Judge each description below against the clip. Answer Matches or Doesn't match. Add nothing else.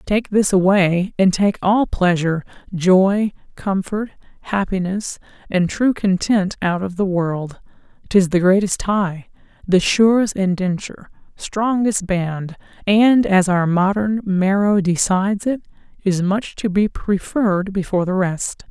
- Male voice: Doesn't match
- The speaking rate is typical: Doesn't match